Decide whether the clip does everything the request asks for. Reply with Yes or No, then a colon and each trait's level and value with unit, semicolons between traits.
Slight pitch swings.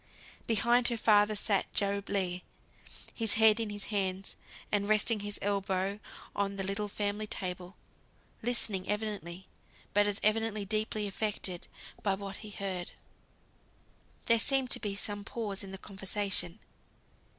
Yes: narrow, 1.6 semitones